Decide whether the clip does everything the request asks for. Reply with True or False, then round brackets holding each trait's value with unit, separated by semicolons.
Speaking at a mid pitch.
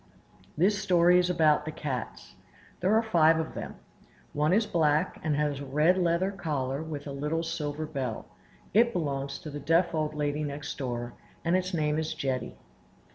True (155 Hz)